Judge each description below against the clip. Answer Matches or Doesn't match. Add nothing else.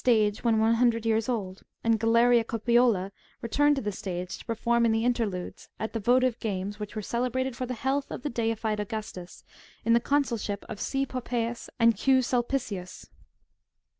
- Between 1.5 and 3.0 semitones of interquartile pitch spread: Matches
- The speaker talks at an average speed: Matches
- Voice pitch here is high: Matches